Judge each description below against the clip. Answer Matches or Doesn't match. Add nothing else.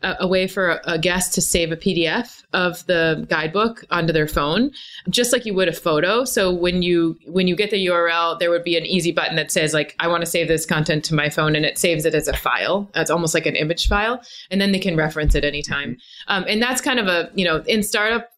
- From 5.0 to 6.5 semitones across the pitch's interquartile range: Doesn't match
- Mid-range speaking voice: Matches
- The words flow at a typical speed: Doesn't match